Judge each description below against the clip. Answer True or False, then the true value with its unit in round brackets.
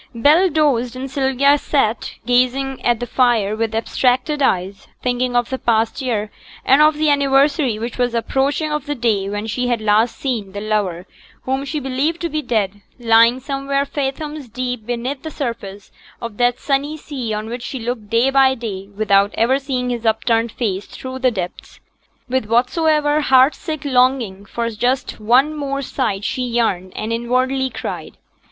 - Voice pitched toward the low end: False (250 Hz)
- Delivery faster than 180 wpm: False (175 wpm)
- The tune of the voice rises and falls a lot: False (3.5 semitones)